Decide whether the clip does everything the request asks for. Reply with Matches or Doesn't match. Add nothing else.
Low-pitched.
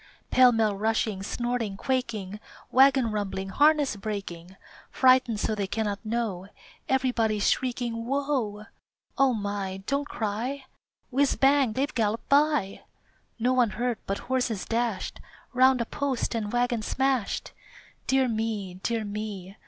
Doesn't match